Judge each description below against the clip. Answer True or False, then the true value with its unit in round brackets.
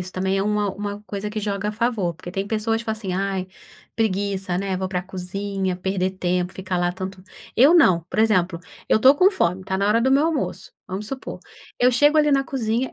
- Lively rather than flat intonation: False (3.1 semitones)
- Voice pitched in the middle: False (200 Hz)